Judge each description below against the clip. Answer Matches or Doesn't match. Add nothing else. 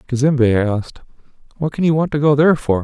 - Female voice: Doesn't match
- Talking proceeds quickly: Matches